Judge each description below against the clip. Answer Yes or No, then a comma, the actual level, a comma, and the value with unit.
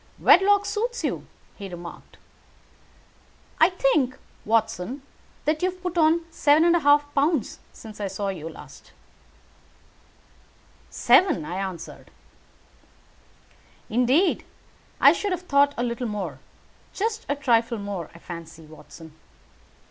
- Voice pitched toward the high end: Yes, very high, 260 Hz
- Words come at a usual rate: No, slow, 120 wpm